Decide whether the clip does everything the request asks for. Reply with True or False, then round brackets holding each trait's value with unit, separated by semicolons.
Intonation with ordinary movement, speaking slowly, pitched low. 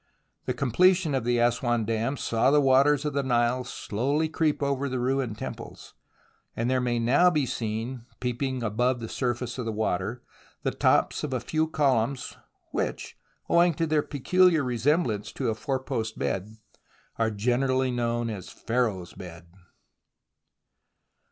False (3.6 semitones; 150 wpm; 125 Hz)